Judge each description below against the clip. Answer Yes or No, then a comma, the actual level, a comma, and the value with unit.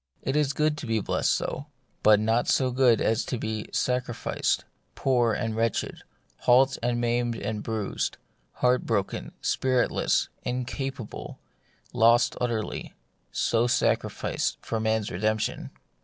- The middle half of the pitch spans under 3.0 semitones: Yes, narrow, 2.4 semitones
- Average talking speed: No, slow, 130 wpm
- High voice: No, low, 120 Hz